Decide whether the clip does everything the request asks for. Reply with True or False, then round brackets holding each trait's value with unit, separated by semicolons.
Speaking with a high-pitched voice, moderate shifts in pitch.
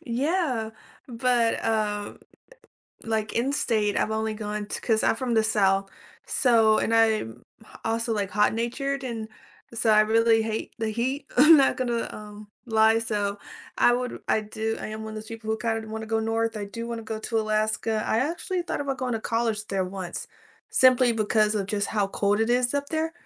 False (225 Hz; 1.8 semitones)